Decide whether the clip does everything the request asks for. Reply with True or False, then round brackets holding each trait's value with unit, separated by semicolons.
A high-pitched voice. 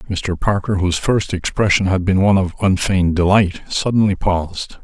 False (95 Hz)